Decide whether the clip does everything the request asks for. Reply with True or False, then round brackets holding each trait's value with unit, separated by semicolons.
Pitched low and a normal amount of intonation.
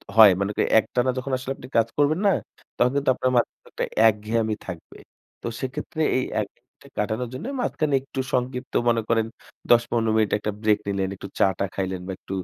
True (115 Hz; 3.6 semitones)